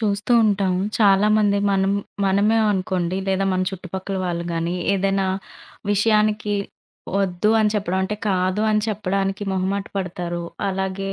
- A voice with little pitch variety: Yes, narrow, 1.8 semitones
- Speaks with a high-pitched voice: Yes, high, 195 Hz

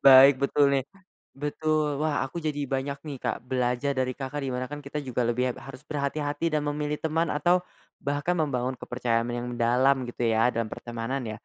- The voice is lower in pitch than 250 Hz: Yes, low, 135 Hz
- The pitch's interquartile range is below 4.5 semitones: Yes, average, 2.8 semitones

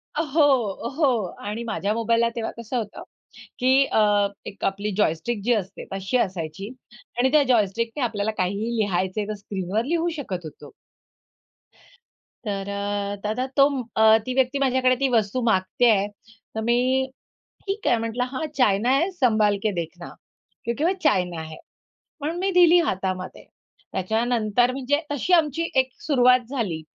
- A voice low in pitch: No, high, 225 Hz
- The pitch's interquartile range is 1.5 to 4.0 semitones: No, average, 4.4 semitones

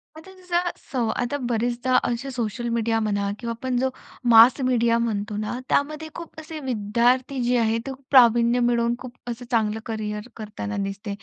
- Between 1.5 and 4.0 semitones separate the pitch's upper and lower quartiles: Yes, average, 2.7 semitones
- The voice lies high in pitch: Yes, high, 235 Hz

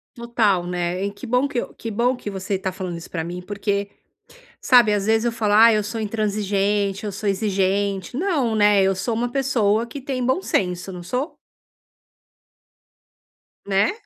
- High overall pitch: Yes, high, 205 Hz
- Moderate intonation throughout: Yes, average, 3.4 semitones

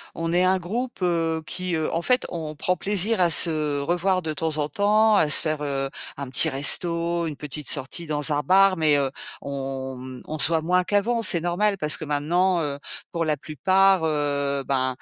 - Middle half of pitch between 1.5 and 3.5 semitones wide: No, average, 3.9 semitones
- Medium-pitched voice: Yes, medium, 160 Hz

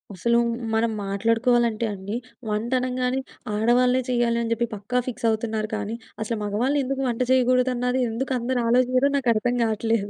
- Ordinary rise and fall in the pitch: No, narrow, 2.2 semitones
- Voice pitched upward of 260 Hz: No, high, 235 Hz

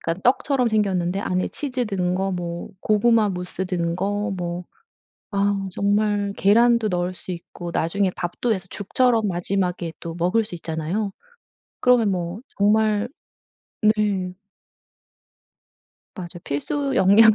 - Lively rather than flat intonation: No, average, 3.3 semitones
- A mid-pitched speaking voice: No, high, 195 Hz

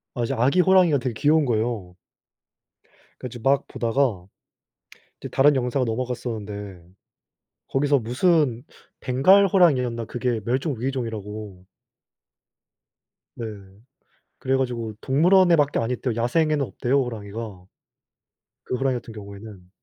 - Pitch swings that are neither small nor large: Yes, average, 3.8 semitones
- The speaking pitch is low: Yes, low, 125 Hz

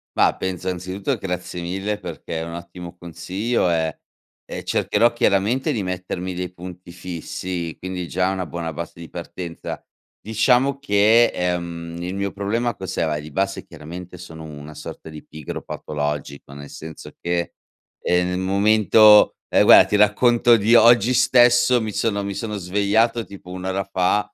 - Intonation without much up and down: No, average, 3.5 semitones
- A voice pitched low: Yes, very low, 95 Hz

